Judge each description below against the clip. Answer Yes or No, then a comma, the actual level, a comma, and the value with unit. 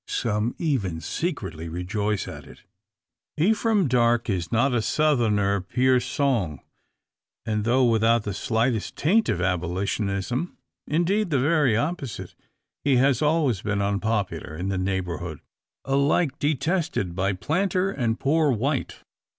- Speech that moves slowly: Yes, slow, 125 wpm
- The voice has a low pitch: Yes, low, 120 Hz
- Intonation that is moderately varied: No, wide, 6.7 semitones